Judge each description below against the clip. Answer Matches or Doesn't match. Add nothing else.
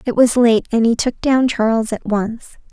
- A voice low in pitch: Doesn't match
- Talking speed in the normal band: Doesn't match